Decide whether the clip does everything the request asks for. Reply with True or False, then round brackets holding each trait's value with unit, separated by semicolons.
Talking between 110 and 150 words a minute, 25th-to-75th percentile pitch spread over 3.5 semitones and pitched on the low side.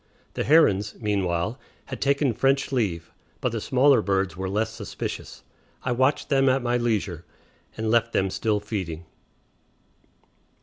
True (140 wpm; 4.9 semitones; 110 Hz)